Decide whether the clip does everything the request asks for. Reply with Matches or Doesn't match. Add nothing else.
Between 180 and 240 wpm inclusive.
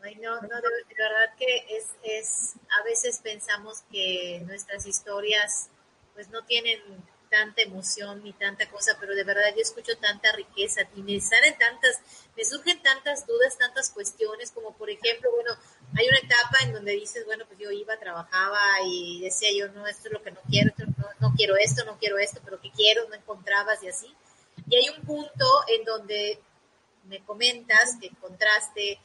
Matches